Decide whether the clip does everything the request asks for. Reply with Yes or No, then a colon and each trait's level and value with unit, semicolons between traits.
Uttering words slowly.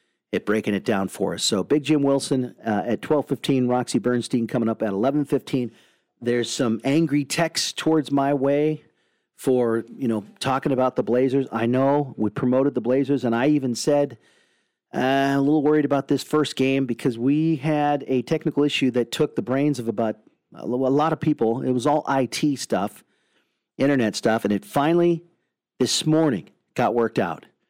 No: average, 180 wpm